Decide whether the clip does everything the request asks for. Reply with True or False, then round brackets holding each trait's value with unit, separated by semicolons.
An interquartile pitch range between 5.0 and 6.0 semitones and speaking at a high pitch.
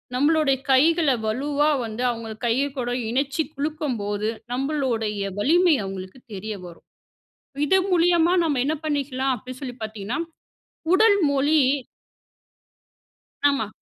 True (5.4 semitones; 270 Hz)